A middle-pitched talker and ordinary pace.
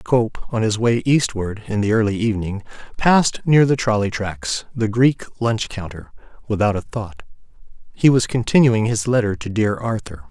No: low, 110 Hz; average, 170 wpm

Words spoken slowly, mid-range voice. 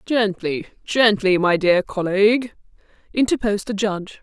No: slow, 115 wpm; high, 205 Hz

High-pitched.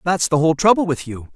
No: medium, 155 Hz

